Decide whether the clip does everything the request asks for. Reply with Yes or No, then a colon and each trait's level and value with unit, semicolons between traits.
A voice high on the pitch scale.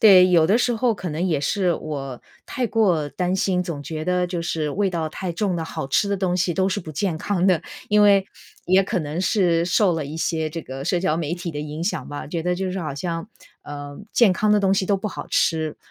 No: medium, 175 Hz